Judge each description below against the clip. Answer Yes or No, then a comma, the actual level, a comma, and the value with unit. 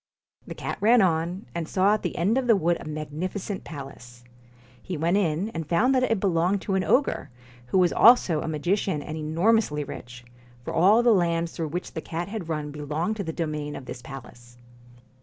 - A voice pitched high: No, medium, 170 Hz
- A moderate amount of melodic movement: Yes, average, 4.6 semitones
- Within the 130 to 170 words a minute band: No, average, 200 wpm